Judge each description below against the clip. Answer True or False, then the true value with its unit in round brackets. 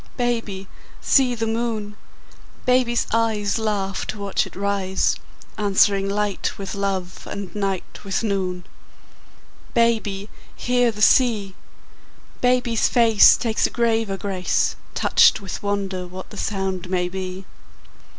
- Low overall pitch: False (205 Hz)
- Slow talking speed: True (120 wpm)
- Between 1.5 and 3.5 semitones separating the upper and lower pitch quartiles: True (2.9 semitones)